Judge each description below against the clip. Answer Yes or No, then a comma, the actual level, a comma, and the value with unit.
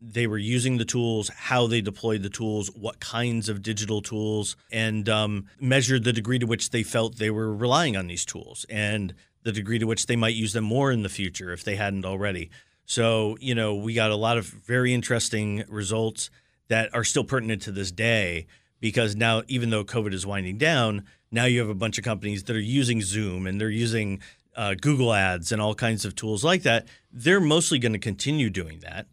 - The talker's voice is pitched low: Yes, low, 110 Hz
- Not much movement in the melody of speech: Yes, narrow, 2.2 semitones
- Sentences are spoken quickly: Yes, fast, 215 wpm